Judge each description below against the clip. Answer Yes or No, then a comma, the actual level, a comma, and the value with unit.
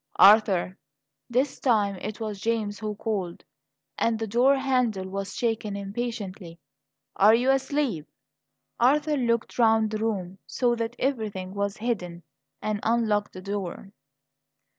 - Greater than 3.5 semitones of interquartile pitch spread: No, average, 3.2 semitones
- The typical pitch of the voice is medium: No, high, 215 Hz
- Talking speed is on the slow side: Yes, slow, 130 wpm